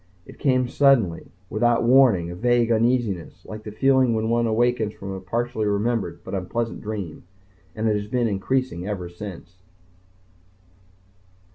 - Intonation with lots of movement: No, average, 3.5 semitones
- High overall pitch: No, low, 110 Hz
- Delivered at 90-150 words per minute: Yes, average, 145 wpm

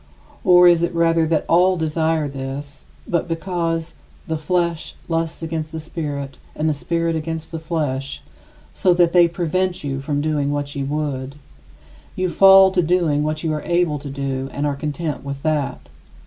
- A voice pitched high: No, medium, 160 Hz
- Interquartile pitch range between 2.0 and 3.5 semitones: Yes, average, 2.9 semitones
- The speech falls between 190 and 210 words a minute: No, average, 175 wpm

